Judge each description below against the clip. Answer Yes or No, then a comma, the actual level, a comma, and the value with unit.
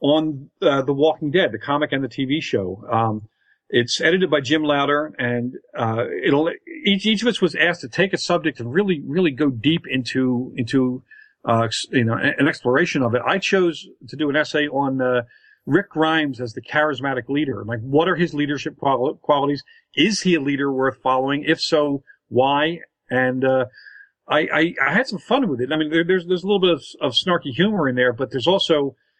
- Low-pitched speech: No, medium, 145 Hz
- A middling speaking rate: No, fast, 210 wpm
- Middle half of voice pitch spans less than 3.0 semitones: No, average, 4.9 semitones